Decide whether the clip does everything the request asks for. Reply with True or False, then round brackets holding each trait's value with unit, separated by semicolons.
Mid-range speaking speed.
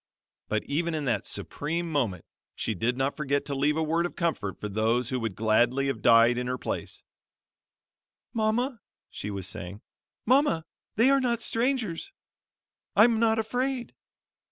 True (155 wpm)